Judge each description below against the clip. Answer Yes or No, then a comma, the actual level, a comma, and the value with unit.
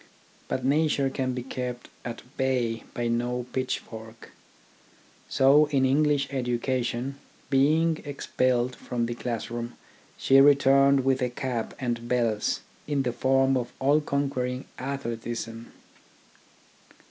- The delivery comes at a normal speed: No, slow, 115 wpm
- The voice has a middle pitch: No, low, 130 Hz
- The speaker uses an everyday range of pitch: No, narrow, 2.3 semitones